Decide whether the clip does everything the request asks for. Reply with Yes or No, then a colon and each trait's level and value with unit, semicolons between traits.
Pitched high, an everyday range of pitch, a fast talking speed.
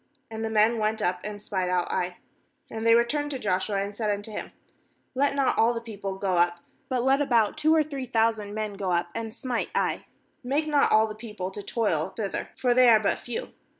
Yes: high, 220 Hz; average, 3.5 semitones; fast, 225 wpm